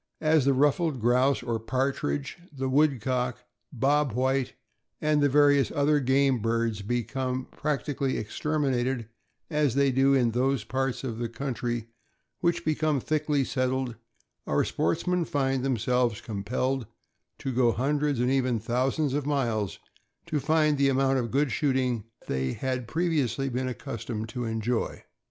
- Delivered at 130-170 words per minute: Yes, average, 150 wpm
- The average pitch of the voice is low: Yes, low, 130 Hz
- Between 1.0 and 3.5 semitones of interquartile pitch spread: Yes, average, 2.8 semitones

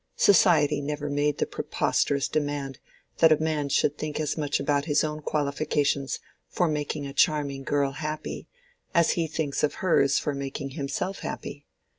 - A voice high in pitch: No, medium, 145 Hz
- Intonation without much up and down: Yes, narrow, 1.5 semitones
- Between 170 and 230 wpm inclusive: No, average, 160 wpm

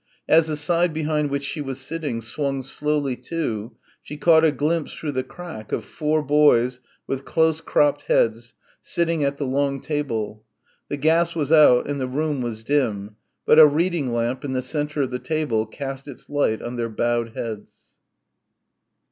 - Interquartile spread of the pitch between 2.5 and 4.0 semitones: Yes, average, 3.7 semitones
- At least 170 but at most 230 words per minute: Yes, average, 175 wpm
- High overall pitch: No, medium, 140 Hz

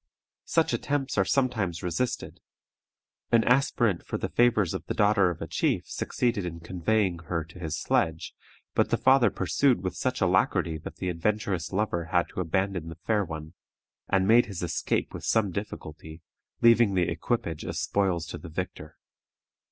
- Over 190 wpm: No, average, 165 wpm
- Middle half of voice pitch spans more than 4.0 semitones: Yes, average, 4.7 semitones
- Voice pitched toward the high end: No, very low, 95 Hz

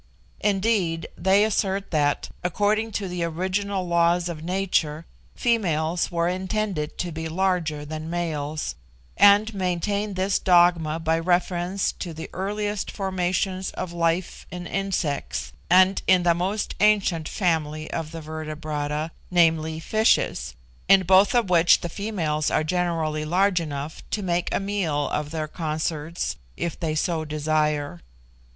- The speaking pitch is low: No, medium, 175 Hz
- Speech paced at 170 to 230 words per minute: No, slow, 135 wpm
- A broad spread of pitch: No, average, 3.4 semitones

